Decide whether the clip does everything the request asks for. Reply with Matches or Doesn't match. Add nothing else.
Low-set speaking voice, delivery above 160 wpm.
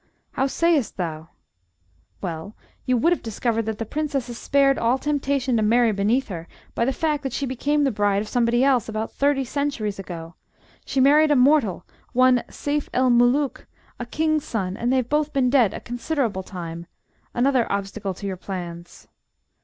Doesn't match